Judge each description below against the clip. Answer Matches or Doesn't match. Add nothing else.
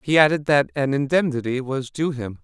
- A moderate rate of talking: Matches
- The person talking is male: Matches